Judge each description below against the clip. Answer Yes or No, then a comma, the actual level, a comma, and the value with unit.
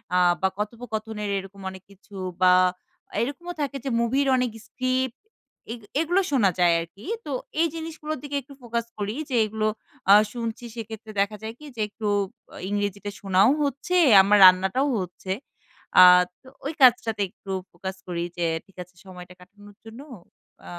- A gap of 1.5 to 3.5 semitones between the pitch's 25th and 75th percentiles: No, average, 4.8 semitones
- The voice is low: No, high, 220 Hz